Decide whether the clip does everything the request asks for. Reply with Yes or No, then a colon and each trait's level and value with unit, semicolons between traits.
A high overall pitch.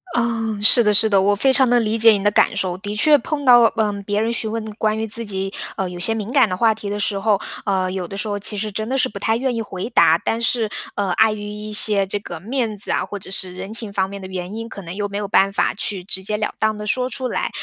Yes: high, 210 Hz